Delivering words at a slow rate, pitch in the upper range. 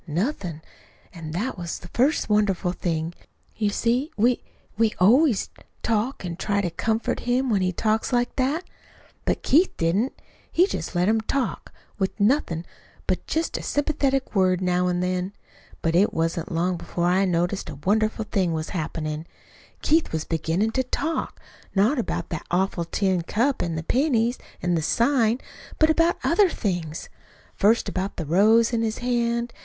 No: average, 165 wpm; high, 205 Hz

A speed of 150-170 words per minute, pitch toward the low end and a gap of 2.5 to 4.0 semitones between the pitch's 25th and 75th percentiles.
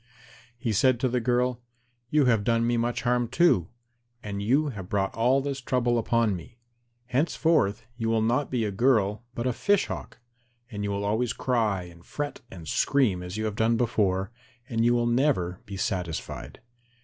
No: average, 185 wpm; low, 115 Hz; average, 3.7 semitones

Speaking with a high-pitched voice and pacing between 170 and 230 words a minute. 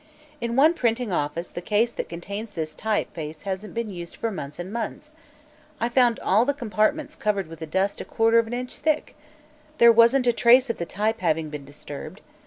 Yes: high, 215 Hz; average, 200 wpm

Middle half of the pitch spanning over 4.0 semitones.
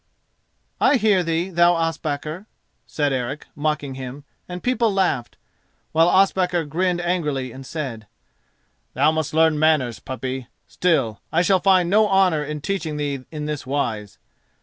Yes: average, 4.4 semitones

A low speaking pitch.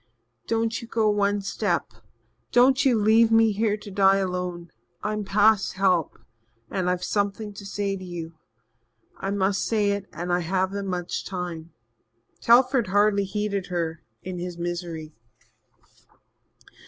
No: high, 195 Hz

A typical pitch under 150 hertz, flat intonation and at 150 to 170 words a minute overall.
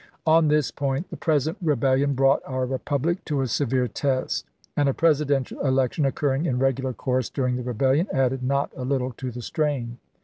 No: low, 135 Hz; narrow, 2.2 semitones; average, 180 wpm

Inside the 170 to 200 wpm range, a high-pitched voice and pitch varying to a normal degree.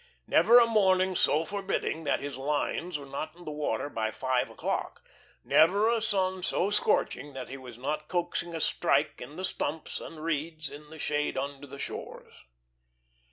No: average, 175 wpm; medium, 155 Hz; average, 4.8 semitones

